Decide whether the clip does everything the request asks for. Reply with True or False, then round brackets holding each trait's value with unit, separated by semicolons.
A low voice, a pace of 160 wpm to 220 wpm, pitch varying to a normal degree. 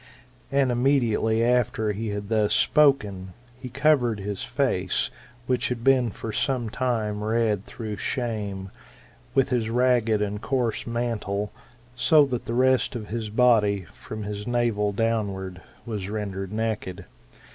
False (115 Hz; 135 wpm; 3.0 semitones)